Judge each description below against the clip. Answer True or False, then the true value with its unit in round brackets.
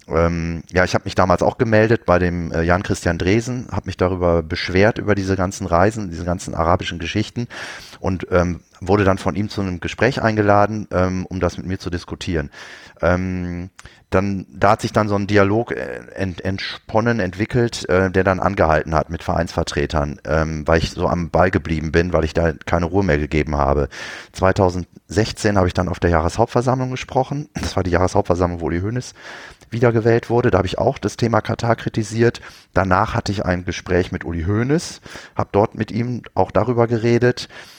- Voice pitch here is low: True (95 Hz)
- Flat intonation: False (3.8 semitones)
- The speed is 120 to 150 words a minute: False (185 wpm)